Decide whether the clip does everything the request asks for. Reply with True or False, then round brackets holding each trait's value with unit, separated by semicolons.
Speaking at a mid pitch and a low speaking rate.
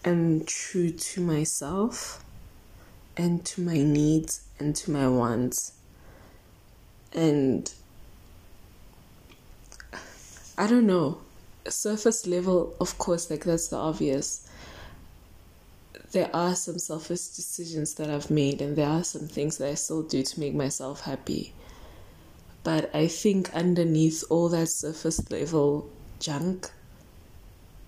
True (145 Hz; 115 wpm)